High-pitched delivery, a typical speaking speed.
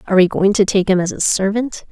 No: high, 195 Hz; fast, 280 wpm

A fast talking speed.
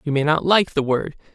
Yes: fast, 265 wpm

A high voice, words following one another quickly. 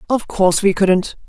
No: high, 195 Hz; average, 190 wpm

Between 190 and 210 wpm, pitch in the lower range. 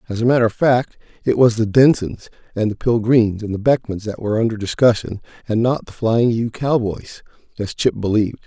Yes: average, 200 wpm; low, 115 Hz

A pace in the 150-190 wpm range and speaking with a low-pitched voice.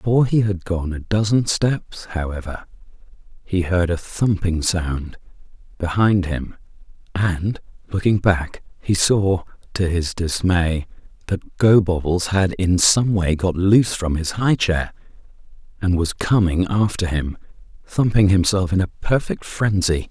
No: slow, 135 wpm; very low, 95 Hz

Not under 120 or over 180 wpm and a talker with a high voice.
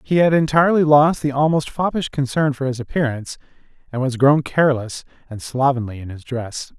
No: average, 175 wpm; low, 135 Hz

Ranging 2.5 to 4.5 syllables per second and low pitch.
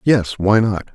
Yes: 3.6 syllables/s; low, 105 Hz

